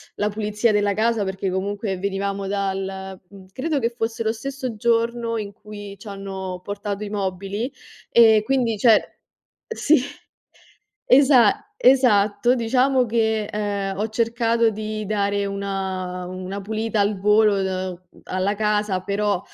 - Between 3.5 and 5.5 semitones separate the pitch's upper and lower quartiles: No, narrow, 2.6 semitones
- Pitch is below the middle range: No, high, 210 Hz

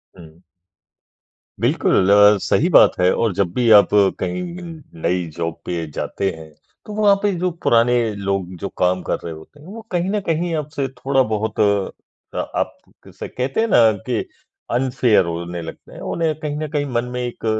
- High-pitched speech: No, low, 115 Hz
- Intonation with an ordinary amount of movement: No, wide, 8.3 semitones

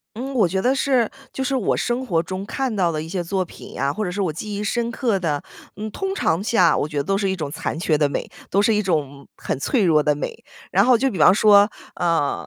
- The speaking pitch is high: Yes, high, 195 Hz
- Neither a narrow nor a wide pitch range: No, wide, 6.0 semitones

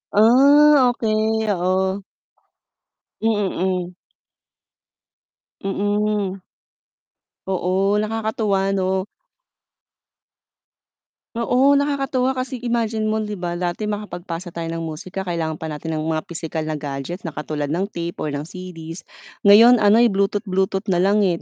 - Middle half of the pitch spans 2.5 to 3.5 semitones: No, average, 4.1 semitones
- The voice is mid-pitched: No, high, 195 Hz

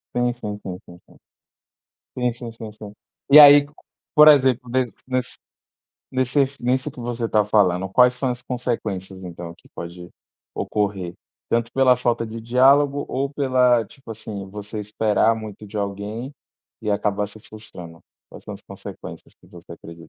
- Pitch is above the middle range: No, low, 115 Hz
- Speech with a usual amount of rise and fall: Yes, average, 3.8 semitones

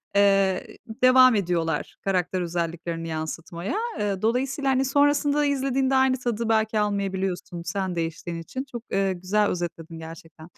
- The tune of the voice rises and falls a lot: Yes, wide, 6.8 semitones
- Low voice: No, high, 195 Hz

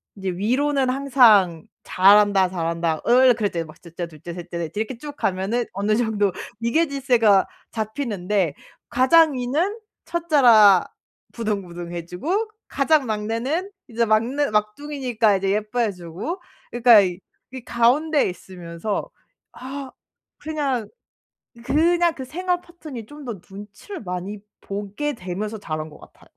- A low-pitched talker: No, high, 225 Hz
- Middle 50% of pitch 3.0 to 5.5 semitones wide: No, wide, 6.2 semitones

